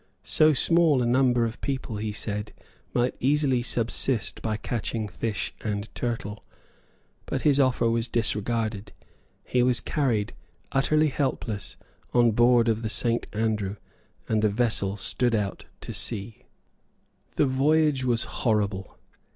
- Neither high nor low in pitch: No, low, 115 Hz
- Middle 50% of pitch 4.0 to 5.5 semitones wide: No, average, 3.3 semitones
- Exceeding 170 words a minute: No, slow, 135 wpm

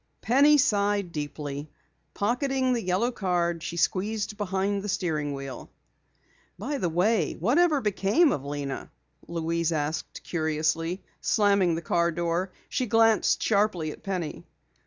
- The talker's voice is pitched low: No, medium, 185 Hz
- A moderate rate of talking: No, slow, 130 wpm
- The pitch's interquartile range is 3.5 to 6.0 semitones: Yes, average, 4.7 semitones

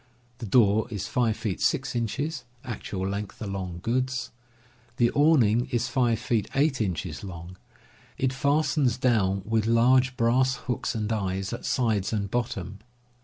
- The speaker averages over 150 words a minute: No, average, 145 wpm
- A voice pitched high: No, low, 115 Hz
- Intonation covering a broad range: No, average, 4.1 semitones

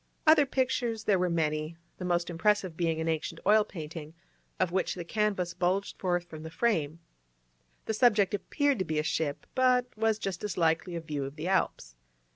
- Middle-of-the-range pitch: Yes, medium, 180 Hz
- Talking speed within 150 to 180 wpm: No, average, 190 wpm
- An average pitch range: Yes, average, 4.6 semitones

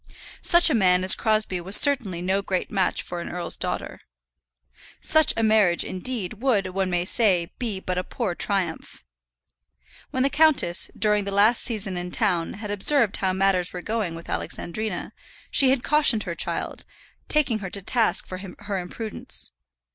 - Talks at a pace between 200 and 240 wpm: No, average, 170 wpm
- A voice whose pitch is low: No, high, 200 Hz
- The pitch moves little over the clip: No, average, 3.9 semitones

